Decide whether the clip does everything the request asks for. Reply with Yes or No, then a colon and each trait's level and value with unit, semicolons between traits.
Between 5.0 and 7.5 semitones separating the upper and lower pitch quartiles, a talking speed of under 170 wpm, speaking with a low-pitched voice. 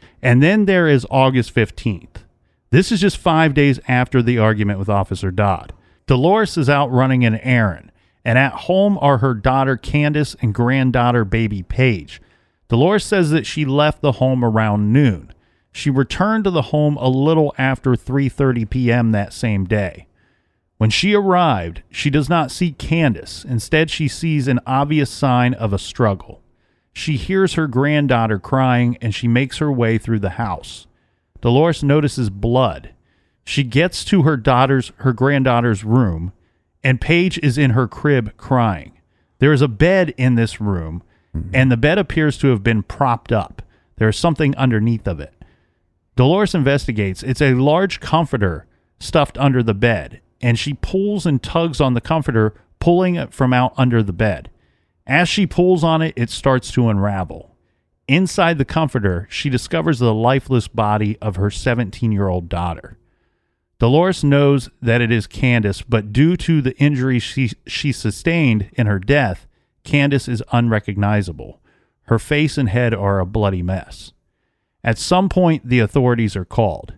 Yes: wide, 5.6 semitones; average, 160 wpm; low, 125 Hz